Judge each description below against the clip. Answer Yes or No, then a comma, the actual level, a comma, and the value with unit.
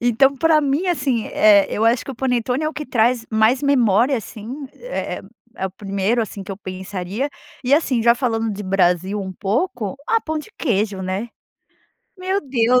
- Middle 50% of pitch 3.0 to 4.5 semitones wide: No, average, 5.3 semitones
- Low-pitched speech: No, high, 235 Hz